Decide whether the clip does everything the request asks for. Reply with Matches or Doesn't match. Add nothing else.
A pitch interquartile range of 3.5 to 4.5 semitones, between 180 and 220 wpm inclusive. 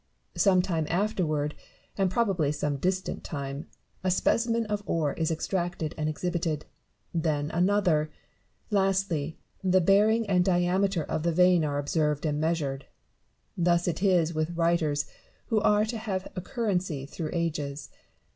Doesn't match